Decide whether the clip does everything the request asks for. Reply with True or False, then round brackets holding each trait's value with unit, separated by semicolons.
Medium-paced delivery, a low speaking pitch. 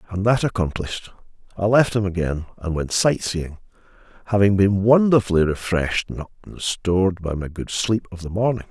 True (170 wpm; 95 Hz)